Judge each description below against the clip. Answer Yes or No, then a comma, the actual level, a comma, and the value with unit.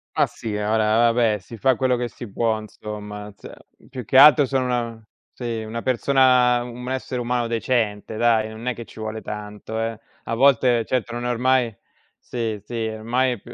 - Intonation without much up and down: Yes, narrow, 2.2 semitones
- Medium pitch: No, low, 115 Hz